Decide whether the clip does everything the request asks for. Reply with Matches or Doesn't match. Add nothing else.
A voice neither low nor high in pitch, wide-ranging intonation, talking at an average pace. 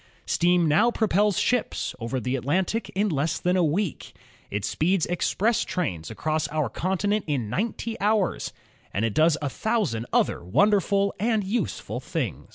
Matches